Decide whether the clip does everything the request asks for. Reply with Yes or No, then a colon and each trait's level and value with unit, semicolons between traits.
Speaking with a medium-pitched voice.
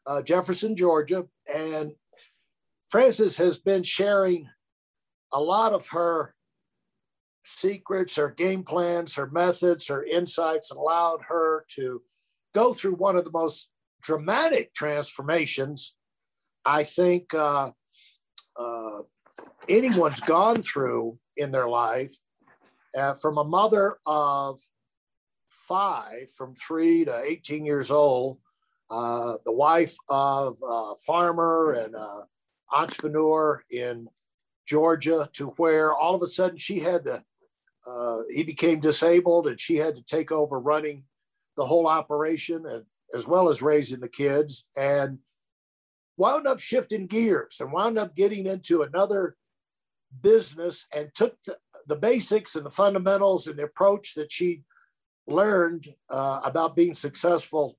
Yes: medium, 160 Hz